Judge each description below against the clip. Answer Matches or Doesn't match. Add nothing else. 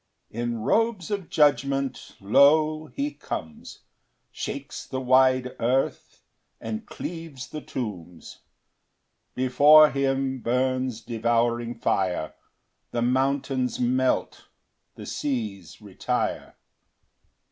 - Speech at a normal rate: Doesn't match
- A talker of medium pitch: Doesn't match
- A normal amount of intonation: Matches